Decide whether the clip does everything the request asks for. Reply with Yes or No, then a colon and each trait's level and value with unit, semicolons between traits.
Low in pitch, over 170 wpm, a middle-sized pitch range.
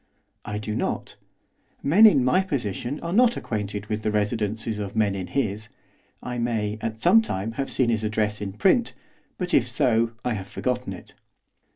Yes: low, 110 Hz; average, 180 wpm; average, 3.5 semitones